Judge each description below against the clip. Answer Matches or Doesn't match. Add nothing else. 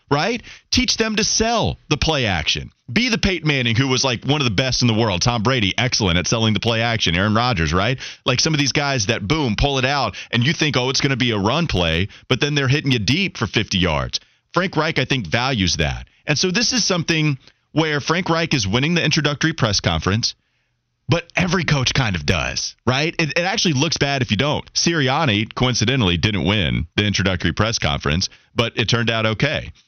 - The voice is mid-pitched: Doesn't match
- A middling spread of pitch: Doesn't match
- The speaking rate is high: Matches